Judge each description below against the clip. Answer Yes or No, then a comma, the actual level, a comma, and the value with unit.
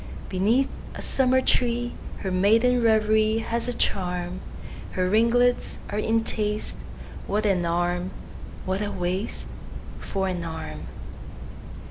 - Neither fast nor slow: No, slow, 95 wpm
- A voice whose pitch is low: No, high, 210 Hz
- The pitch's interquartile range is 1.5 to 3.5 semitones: No, average, 4.1 semitones